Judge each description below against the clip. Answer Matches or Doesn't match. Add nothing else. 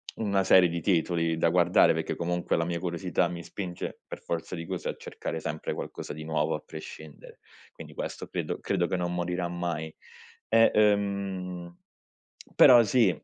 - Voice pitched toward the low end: Matches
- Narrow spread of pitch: Matches